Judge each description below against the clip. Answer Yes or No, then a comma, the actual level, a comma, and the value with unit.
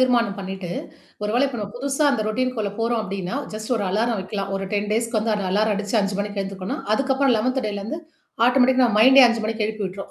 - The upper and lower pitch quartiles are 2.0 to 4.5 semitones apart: Yes, average, 3.7 semitones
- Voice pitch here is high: Yes, high, 215 Hz